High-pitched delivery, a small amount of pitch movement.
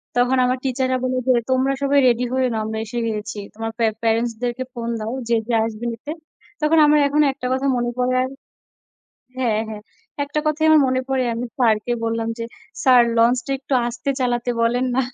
Yes: high, 245 Hz; narrow, 2.3 semitones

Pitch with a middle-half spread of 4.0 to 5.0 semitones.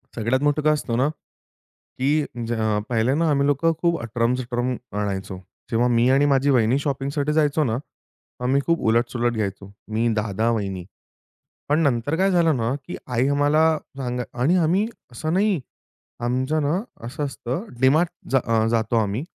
Yes: average, 4.3 semitones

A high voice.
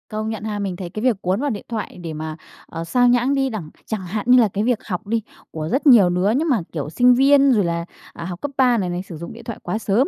Yes: high, 215 Hz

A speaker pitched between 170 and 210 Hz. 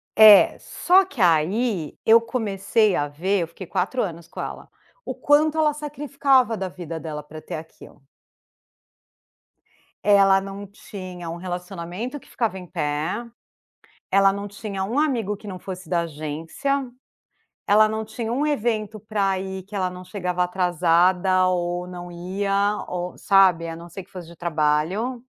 Yes: high, 190 Hz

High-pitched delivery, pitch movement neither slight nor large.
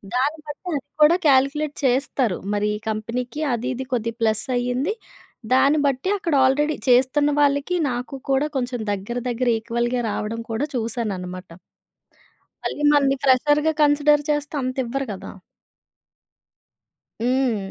Yes: very high, 255 Hz; average, 3.6 semitones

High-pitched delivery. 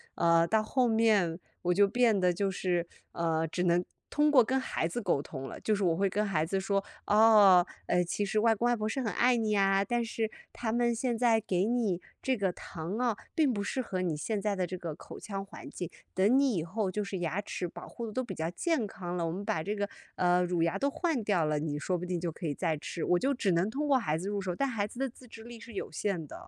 Yes: high, 200 Hz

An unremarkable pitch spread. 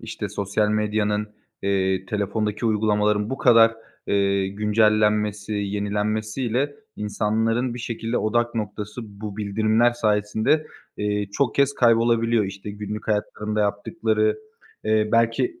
No: narrow, 1.7 semitones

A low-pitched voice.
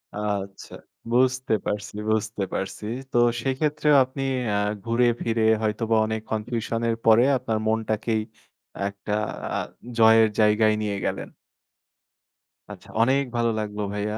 Yes: low, 110 Hz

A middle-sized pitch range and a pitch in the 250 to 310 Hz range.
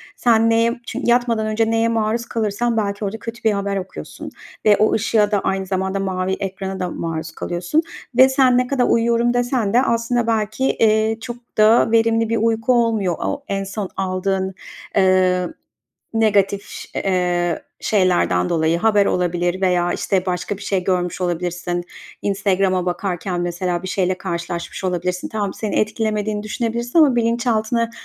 No: average, 3.6 semitones; high, 200 Hz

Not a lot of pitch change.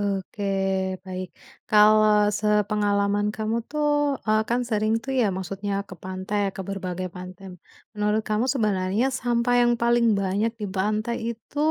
Yes: narrow, 2.3 semitones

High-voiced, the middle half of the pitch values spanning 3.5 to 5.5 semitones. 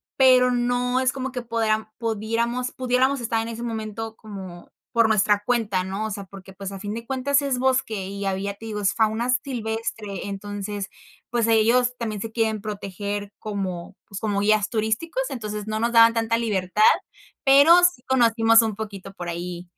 No: high, 220 Hz; average, 2.9 semitones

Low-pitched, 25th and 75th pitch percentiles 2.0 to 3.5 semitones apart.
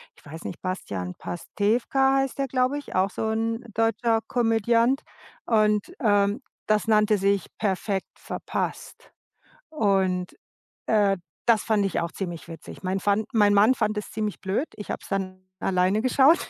No: high, 210 Hz; average, 3.0 semitones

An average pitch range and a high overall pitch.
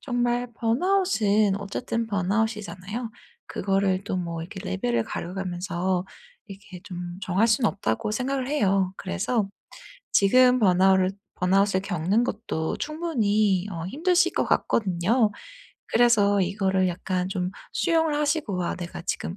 Yes: average, 4.3 semitones; high, 200 Hz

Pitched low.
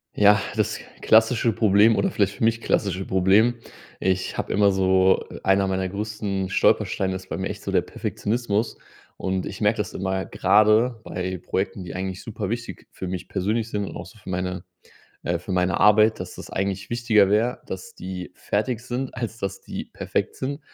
Yes: low, 100 Hz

